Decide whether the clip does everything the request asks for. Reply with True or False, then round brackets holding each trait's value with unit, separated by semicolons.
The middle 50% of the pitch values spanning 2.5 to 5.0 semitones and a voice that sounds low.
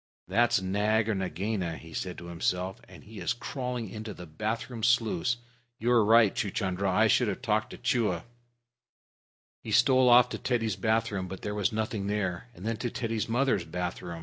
True (3.6 semitones; 110 Hz)